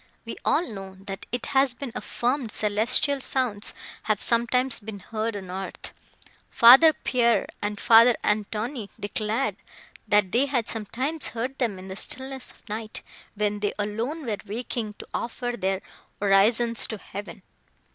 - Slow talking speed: No, average, 145 wpm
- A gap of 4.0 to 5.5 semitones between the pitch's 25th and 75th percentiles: No, average, 3.4 semitones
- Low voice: No, high, 225 Hz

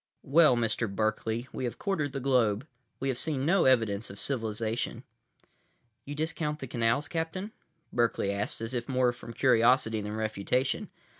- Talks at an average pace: Yes, average, 155 wpm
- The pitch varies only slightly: No, average, 3.8 semitones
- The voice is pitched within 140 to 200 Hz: No, low, 120 Hz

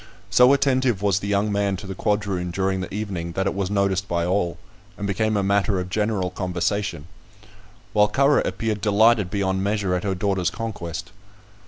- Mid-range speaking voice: No, low, 100 Hz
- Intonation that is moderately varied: No, narrow, 2.1 semitones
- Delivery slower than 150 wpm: No, average, 180 wpm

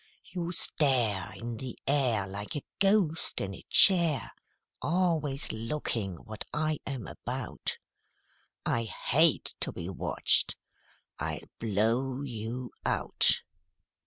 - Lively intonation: Yes, wide, 5.7 semitones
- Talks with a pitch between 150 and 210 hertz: No, low, 130 Hz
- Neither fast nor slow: No, slow, 110 wpm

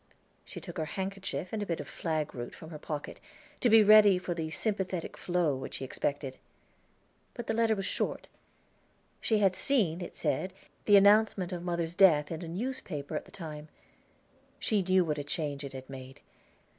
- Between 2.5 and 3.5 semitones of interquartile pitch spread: No, average, 4.8 semitones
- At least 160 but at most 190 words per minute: Yes, average, 180 wpm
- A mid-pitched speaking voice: Yes, medium, 175 Hz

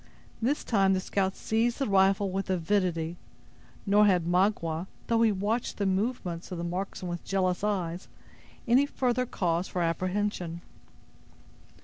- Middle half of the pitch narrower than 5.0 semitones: Yes, average, 2.9 semitones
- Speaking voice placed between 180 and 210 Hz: Yes, high, 190 Hz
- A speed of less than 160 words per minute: Yes, average, 140 wpm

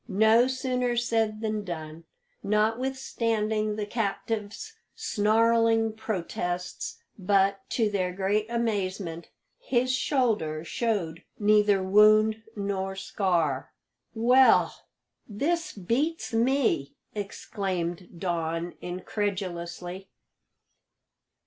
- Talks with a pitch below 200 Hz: No, high, 210 Hz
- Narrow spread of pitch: No, average, 3.6 semitones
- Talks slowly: Yes, slow, 80 wpm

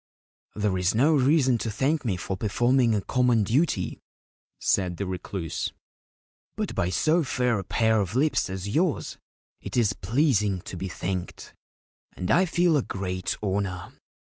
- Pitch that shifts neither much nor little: No, wide, 5.9 semitones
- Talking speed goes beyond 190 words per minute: No, average, 160 wpm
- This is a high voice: No, low, 110 Hz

